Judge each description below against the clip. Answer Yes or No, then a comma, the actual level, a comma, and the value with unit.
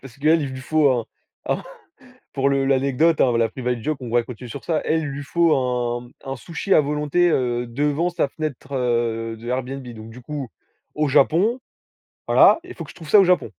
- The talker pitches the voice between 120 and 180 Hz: Yes, low, 135 Hz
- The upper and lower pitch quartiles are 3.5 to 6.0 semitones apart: Yes, average, 4.0 semitones